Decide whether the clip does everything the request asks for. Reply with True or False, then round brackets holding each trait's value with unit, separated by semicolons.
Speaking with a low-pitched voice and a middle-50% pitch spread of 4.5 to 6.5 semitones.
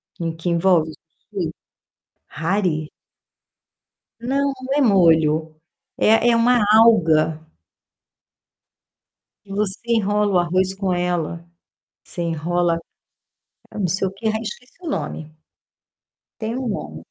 False (185 Hz; 5.0 semitones)